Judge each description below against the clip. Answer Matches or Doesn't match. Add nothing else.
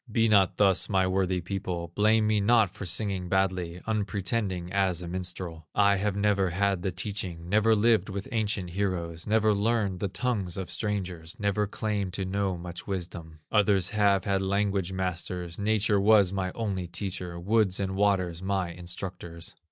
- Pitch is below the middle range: Matches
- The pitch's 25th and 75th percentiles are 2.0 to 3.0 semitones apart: Matches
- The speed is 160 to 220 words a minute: Matches